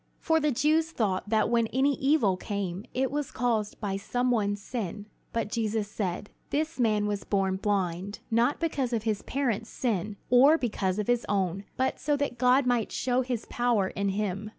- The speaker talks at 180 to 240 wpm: Yes, average, 185 wpm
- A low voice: No, high, 225 Hz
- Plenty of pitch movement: No, average, 4.0 semitones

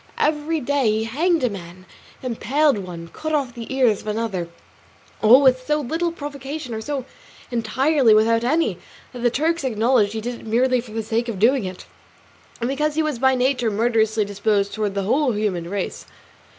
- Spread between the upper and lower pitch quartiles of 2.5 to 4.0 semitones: No, average, 4.6 semitones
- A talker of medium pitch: No, high, 240 Hz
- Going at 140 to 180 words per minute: No, average, 190 wpm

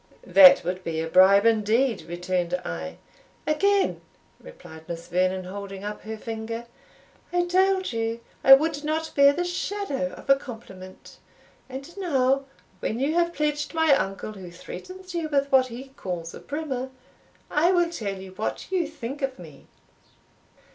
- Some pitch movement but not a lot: No, wide, 8.6 semitones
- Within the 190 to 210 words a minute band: No, average, 155 wpm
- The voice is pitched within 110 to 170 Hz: No, very high, 255 Hz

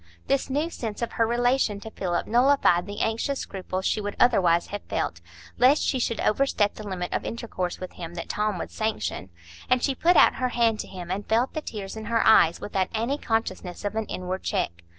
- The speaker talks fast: Yes, fast, 210 wpm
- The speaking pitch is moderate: No, high, 215 Hz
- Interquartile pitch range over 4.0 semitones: Yes, average, 4.4 semitones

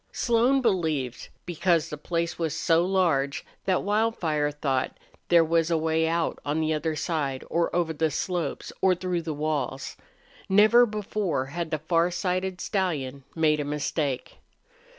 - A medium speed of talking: Yes, average, 150 wpm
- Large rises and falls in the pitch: No, average, 3.4 semitones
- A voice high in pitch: No, medium, 165 Hz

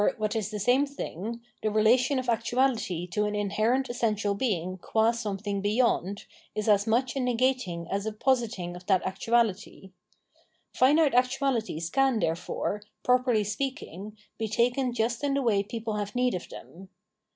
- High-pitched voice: Yes, high, 220 Hz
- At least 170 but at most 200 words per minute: No, average, 155 wpm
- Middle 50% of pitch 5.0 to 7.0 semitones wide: No, average, 3.7 semitones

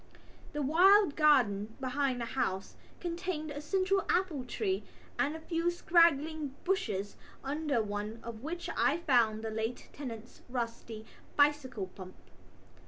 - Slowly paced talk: Yes, slow, 130 wpm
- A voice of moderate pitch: No, very high, 280 Hz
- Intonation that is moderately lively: No, wide, 6.5 semitones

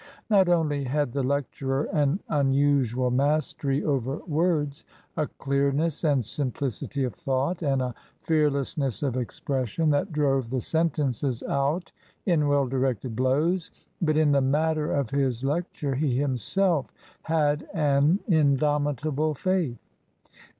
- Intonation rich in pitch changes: No, narrow, 2.5 semitones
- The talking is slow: Yes, slow, 130 wpm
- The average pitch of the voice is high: No, medium, 145 Hz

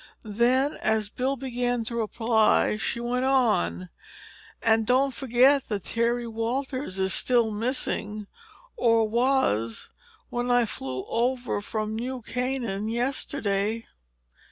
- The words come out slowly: Yes, slow, 110 wpm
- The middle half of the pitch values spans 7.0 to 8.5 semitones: No, average, 2.9 semitones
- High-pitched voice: Yes, high, 235 Hz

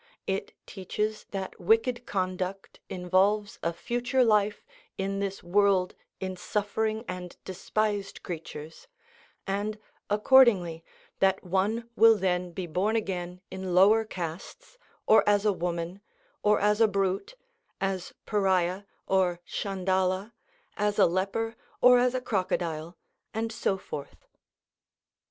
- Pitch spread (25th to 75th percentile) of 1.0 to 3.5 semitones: Yes, average, 2.7 semitones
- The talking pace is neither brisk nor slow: No, slow, 120 wpm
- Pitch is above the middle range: Yes, high, 195 Hz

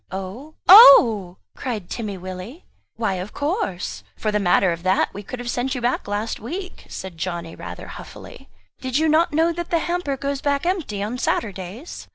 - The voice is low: No, high, 235 Hz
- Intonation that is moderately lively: No, wide, 7.7 semitones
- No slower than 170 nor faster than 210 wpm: Yes, average, 185 wpm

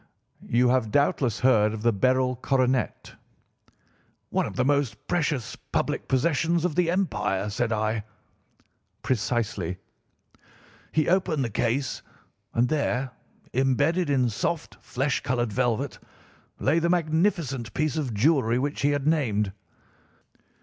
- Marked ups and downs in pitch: No, average, 4.4 semitones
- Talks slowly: Yes, slow, 125 wpm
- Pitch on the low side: Yes, low, 130 Hz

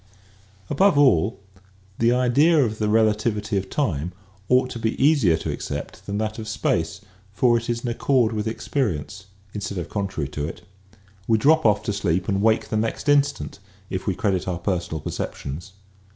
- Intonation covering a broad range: No, average, 4.0 semitones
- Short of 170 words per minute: No, average, 175 wpm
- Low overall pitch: Yes, low, 110 Hz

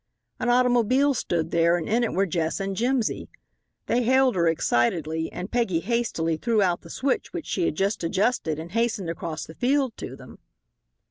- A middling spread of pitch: No, wide, 6.6 semitones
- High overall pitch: Yes, high, 195 Hz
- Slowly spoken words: No, average, 185 wpm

